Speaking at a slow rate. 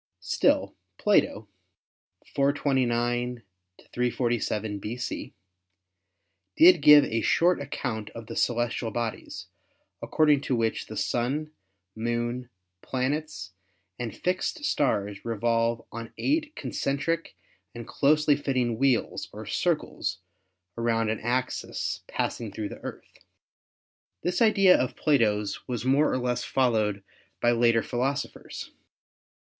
Yes: slow, 105 wpm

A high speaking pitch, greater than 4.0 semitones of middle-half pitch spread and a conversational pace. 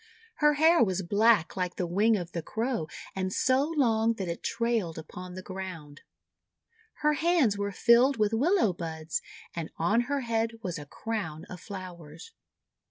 Yes: high, 200 Hz; average, 5.2 semitones; average, 165 wpm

